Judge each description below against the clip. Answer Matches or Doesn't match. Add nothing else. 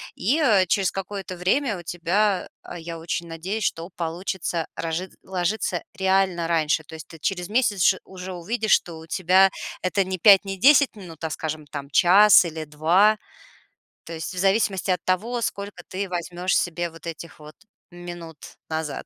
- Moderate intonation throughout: Matches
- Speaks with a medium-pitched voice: Matches